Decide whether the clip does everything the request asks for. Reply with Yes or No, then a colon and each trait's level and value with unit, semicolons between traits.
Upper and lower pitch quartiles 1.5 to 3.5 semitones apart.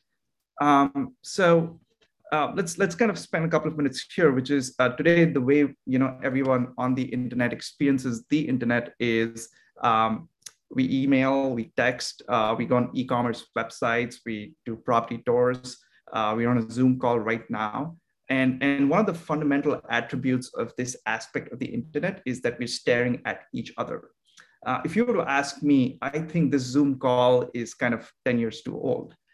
Yes: average, 2.9 semitones